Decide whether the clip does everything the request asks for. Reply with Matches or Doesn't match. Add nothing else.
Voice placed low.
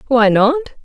Doesn't match